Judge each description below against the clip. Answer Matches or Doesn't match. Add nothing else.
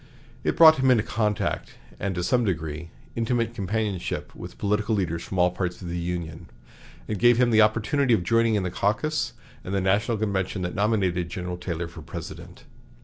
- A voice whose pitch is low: Matches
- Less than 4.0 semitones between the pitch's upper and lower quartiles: Doesn't match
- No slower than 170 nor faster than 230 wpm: Matches